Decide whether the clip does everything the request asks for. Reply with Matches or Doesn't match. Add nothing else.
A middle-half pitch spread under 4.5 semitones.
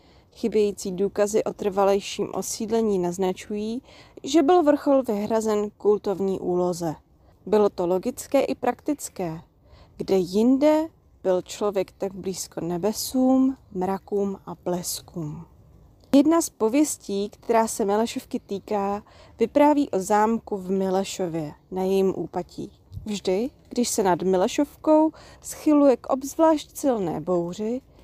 Doesn't match